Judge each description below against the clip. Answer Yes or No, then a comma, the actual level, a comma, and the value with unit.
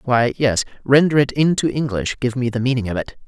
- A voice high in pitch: No, low, 125 Hz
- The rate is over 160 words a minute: Yes, average, 200 wpm